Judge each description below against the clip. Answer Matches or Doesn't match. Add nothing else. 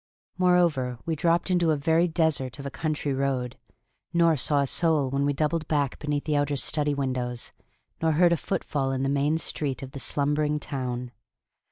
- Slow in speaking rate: Doesn't match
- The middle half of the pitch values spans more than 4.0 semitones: Doesn't match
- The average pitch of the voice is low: Doesn't match